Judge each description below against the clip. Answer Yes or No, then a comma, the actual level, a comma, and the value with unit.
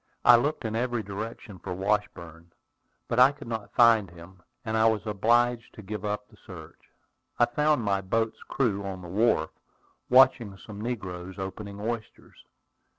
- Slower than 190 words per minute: Yes, average, 160 wpm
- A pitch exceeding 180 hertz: No, low, 110 Hz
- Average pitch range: Yes, average, 3.4 semitones